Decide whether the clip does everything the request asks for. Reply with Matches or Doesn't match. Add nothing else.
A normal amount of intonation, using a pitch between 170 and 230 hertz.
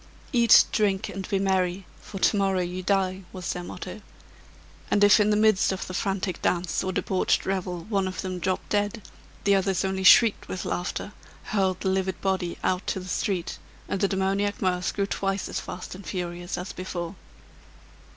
Doesn't match